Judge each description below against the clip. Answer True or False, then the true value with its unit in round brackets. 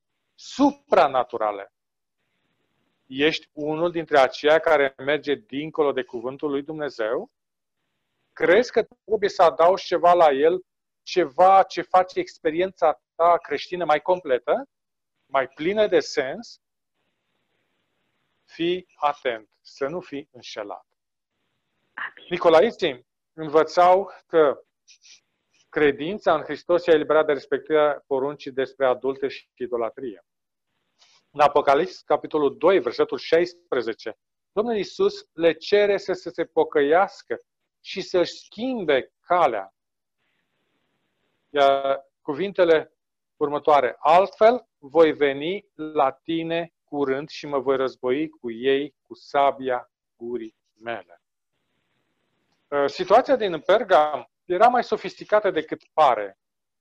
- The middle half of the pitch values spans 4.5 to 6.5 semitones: True (5.2 semitones)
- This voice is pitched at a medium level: True (160 Hz)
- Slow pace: True (100 wpm)